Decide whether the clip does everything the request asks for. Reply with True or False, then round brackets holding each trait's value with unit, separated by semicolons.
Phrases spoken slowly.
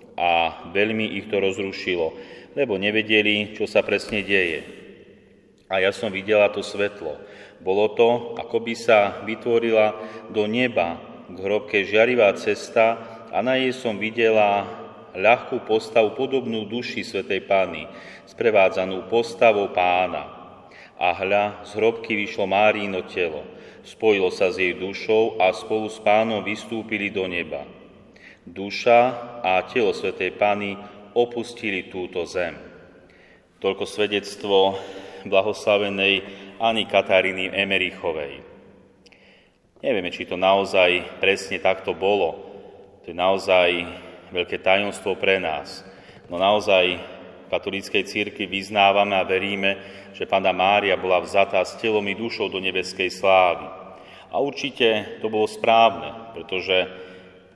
False (120 wpm)